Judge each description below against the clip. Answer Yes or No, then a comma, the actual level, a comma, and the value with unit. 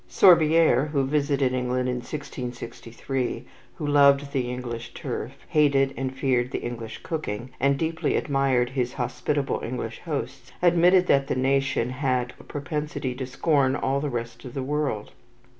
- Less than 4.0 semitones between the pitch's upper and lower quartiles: Yes, narrow, 2.6 semitones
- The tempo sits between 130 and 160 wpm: Yes, average, 150 wpm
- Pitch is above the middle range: No, low, 135 Hz